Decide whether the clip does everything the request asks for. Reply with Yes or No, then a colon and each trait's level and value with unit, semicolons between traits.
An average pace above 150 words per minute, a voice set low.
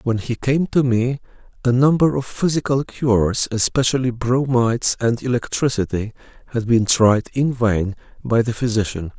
No: average, 145 wpm; low, 120 Hz